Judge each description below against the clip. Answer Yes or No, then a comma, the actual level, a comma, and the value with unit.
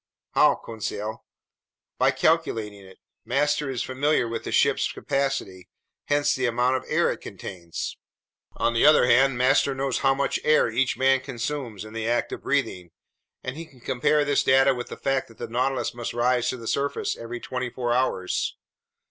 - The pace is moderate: Yes, average, 180 wpm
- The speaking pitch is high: No, low, 125 Hz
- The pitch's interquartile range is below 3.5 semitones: Yes, average, 2.8 semitones